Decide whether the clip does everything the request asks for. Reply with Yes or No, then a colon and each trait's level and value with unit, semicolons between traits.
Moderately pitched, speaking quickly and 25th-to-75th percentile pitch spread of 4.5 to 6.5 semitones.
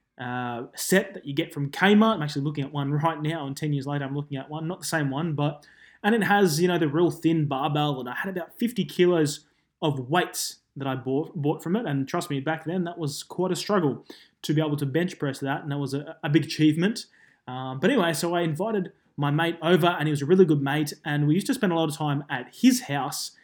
No: medium, 155 Hz; fast, 260 wpm; average, 3.7 semitones